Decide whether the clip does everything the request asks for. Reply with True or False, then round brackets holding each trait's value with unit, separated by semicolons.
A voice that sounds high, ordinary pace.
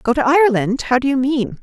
False (250 Hz; 220 wpm)